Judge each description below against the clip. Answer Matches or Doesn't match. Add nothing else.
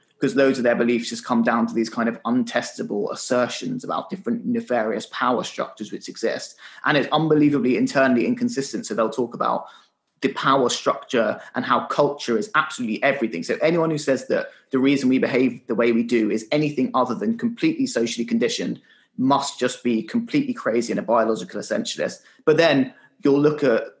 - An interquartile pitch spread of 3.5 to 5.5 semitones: Matches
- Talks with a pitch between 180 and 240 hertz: Doesn't match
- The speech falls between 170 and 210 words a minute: Matches